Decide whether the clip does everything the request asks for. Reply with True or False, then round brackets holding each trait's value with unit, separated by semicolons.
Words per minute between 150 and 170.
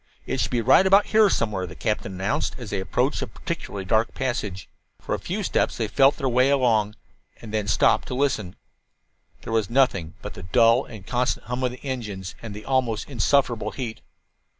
False (195 wpm)